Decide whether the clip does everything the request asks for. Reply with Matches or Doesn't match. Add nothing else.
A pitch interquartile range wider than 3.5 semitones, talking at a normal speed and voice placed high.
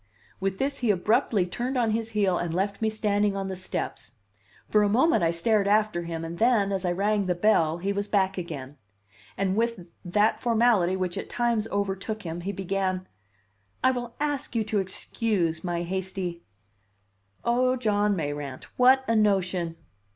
Matches